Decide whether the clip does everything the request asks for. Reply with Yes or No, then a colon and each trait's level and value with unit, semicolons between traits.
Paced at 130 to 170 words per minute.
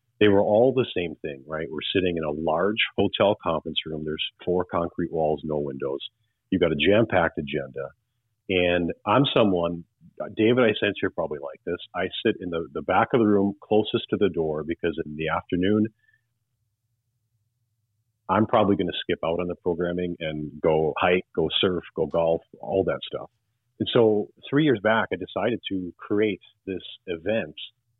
No: average, 180 wpm